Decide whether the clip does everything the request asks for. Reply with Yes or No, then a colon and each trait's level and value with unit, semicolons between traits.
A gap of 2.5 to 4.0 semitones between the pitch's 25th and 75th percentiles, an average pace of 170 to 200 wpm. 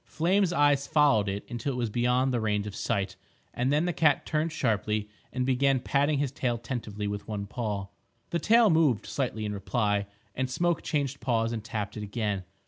No: average, 5.3 semitones; average, 195 wpm